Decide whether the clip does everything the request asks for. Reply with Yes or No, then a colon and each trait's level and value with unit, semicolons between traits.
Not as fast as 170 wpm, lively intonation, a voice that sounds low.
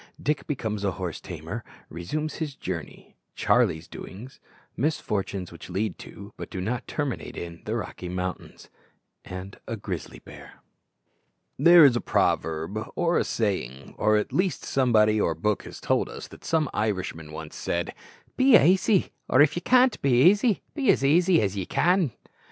Yes: average, 160 wpm; wide, 9.0 semitones; low, 110 Hz